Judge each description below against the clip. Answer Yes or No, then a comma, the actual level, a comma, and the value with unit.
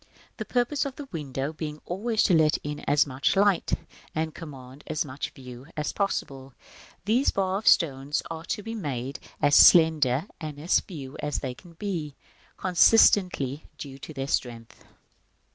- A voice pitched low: No, medium, 150 Hz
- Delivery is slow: No, average, 170 wpm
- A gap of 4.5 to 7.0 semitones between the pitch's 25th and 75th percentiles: Yes, wide, 5.5 semitones